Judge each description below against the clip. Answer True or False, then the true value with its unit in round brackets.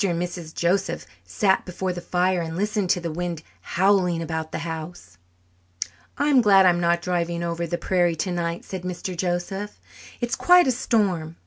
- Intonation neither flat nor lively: False (2.2 semitones)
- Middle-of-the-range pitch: True (175 Hz)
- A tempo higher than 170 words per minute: False (165 wpm)